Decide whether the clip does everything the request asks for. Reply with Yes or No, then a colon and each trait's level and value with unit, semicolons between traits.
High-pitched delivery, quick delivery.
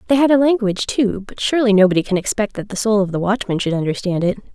Yes: high, 210 Hz; fast, 250 wpm